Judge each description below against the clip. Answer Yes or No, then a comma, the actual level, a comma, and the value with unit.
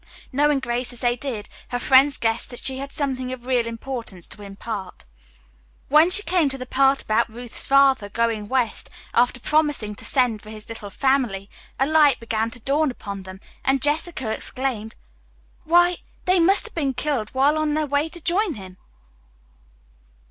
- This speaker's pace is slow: No, average, 175 wpm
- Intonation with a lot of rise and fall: No, average, 4.5 semitones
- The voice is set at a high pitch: Yes, very high, 260 Hz